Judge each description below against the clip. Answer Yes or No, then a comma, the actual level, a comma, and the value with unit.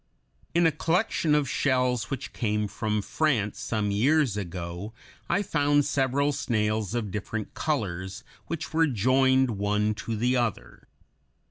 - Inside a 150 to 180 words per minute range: No, slow, 135 wpm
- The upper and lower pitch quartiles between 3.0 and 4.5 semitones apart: No, wide, 5.5 semitones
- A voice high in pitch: No, low, 120 Hz